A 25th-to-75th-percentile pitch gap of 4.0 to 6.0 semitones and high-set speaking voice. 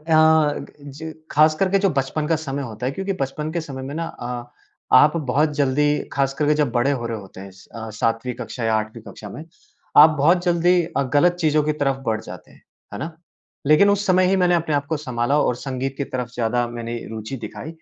No: average, 4.5 semitones; medium, 145 Hz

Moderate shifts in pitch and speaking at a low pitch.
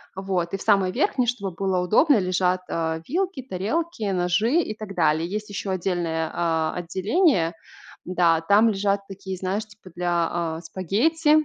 No: average, 3.7 semitones; high, 190 Hz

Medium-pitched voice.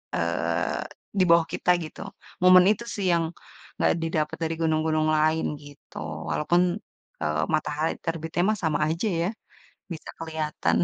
Yes: medium, 160 Hz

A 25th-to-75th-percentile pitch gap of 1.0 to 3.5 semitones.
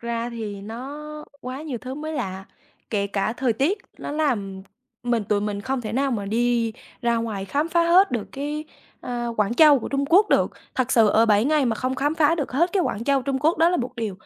No: average, 4.7 semitones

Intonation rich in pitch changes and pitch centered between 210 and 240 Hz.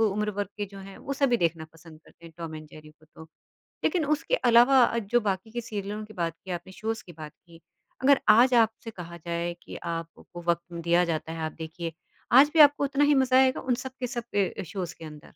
No: wide, 6.3 semitones; high, 195 Hz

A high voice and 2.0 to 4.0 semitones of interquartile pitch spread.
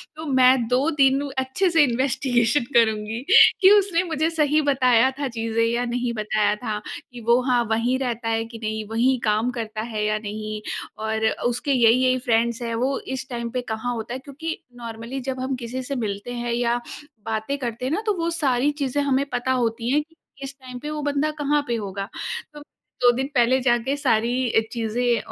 Yes: high, 245 Hz; average, 2.9 semitones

